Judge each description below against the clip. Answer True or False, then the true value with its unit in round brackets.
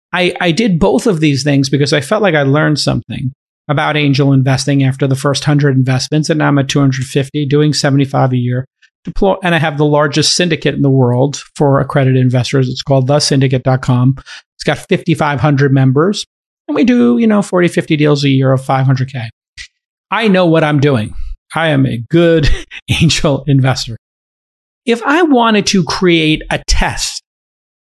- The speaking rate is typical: True (170 wpm)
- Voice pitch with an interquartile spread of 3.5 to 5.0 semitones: True (4.0 semitones)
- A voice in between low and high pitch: True (145 Hz)